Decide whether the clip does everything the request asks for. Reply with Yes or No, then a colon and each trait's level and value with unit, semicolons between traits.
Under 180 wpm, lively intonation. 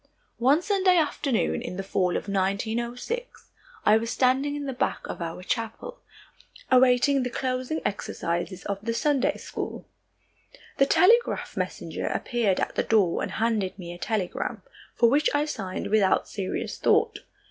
Yes: average, 150 wpm; wide, 5.9 semitones